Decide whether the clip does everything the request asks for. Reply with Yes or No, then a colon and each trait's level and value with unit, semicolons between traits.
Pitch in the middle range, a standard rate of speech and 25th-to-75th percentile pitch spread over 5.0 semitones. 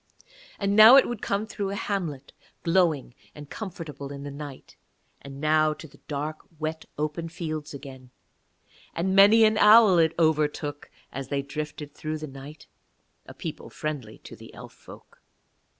No: medium, 155 Hz; average, 160 wpm; average, 4.7 semitones